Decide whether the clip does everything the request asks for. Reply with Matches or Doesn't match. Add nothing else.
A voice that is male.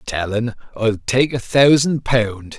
Matches